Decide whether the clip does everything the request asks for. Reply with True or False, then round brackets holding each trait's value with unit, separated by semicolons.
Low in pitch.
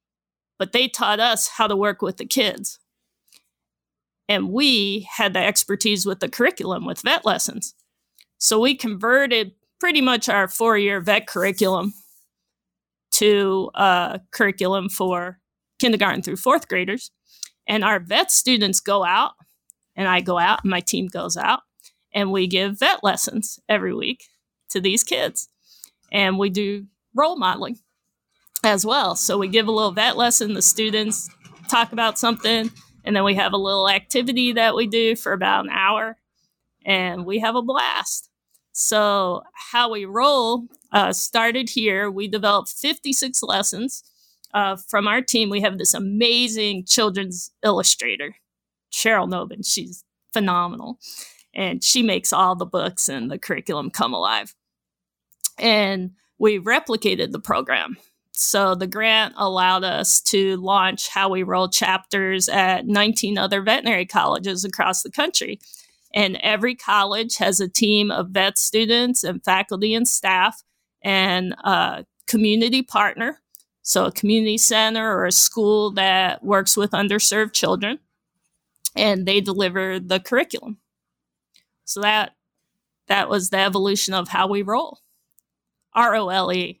False (205 Hz)